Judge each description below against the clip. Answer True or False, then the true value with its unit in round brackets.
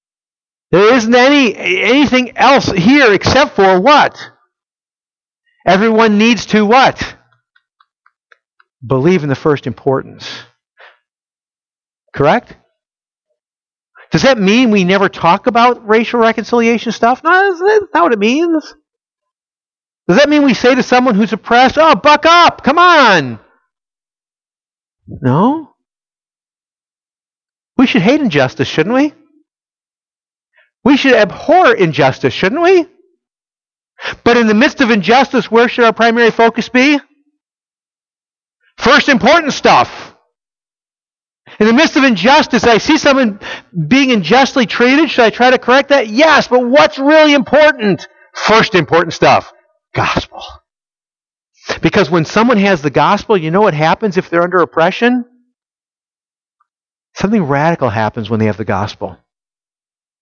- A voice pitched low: False (240 Hz)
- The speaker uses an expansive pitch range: True (6.5 semitones)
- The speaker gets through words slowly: True (125 wpm)